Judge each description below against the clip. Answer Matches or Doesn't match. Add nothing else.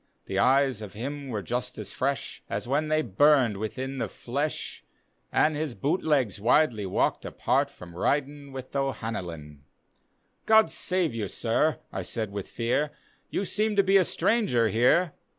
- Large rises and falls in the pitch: Matches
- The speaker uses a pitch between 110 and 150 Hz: Matches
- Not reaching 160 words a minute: Doesn't match